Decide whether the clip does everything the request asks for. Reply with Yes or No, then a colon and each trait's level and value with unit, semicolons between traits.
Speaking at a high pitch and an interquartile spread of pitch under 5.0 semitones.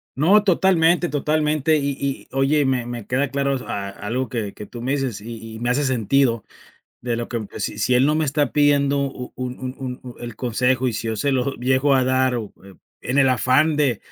No: low, 130 Hz; average, 3.0 semitones